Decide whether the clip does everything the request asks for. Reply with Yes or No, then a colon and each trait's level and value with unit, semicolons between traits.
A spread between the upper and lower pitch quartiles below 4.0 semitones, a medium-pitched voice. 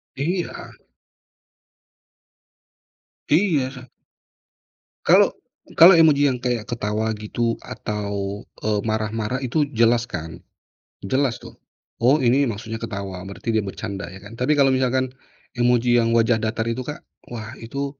No: average, 3.5 semitones; low, 120 Hz